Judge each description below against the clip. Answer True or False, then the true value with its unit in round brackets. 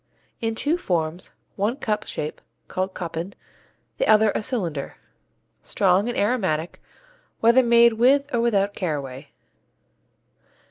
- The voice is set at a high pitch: True (205 Hz)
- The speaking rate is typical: False (120 wpm)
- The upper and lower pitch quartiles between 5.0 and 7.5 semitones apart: True (5.3 semitones)